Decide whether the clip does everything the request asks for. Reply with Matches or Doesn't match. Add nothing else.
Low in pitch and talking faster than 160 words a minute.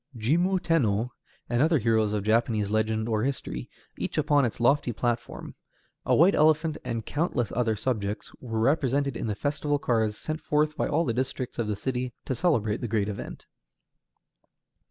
Matches